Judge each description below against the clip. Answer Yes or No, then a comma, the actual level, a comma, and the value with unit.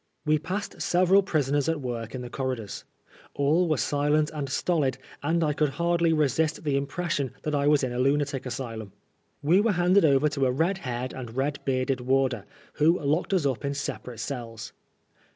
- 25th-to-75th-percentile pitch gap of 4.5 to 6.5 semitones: No, average, 3.7 semitones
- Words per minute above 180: Yes, average, 190 wpm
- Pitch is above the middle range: No, medium, 145 Hz